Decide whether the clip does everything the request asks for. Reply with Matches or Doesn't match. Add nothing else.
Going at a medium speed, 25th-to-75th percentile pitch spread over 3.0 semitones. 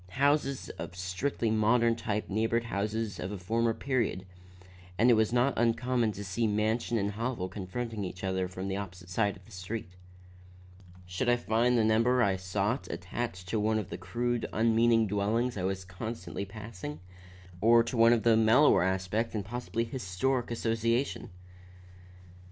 Matches